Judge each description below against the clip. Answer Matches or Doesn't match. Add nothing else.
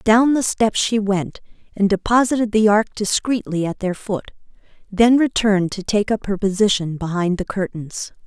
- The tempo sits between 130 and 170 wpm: Matches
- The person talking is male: Doesn't match